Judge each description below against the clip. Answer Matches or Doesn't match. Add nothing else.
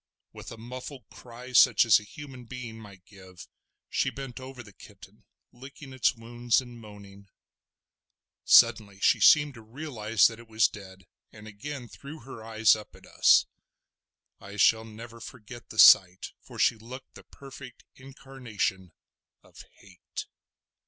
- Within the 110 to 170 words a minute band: Matches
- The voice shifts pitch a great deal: Doesn't match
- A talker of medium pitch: Doesn't match